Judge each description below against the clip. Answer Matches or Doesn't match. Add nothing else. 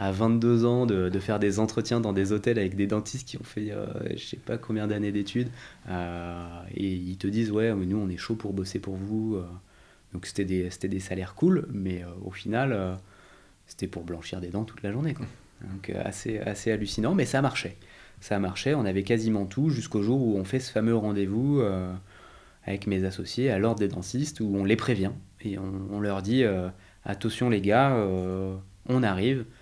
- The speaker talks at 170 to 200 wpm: Doesn't match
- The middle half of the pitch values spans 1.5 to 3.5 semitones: Matches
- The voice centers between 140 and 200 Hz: Doesn't match